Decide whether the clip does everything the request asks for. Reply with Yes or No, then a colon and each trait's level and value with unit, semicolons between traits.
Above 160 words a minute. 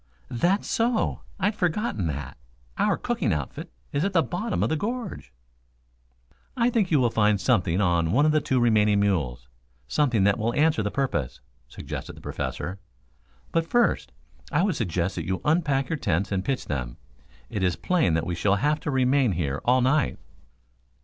Yes: average, 175 wpm